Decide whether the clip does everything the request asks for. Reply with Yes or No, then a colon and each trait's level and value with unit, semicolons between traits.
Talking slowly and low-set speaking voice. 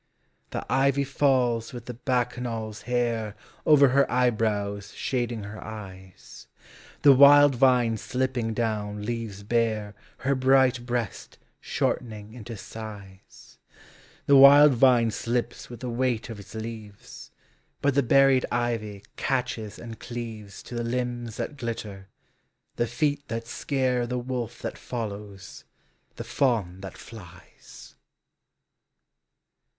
Yes: slow, 120 wpm; low, 120 Hz